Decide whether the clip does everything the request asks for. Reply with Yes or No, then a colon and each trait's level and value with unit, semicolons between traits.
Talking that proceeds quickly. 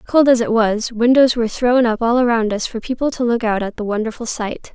Yes: fast, 255 wpm